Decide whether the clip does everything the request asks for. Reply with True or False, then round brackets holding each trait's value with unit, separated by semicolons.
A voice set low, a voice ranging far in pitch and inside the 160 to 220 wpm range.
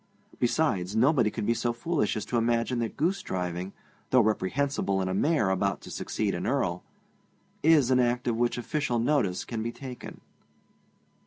False (120 Hz; 4.4 semitones; 165 wpm)